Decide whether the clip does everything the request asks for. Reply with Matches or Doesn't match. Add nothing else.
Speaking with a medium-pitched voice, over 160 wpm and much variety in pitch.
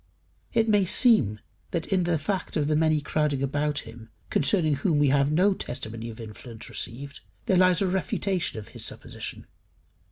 Matches